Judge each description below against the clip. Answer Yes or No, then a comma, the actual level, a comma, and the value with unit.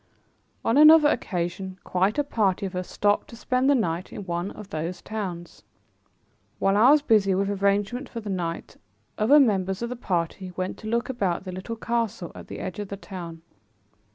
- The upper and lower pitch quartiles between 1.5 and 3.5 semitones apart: No, average, 4.0 semitones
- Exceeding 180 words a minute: Yes, average, 190 wpm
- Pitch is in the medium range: No, high, 200 Hz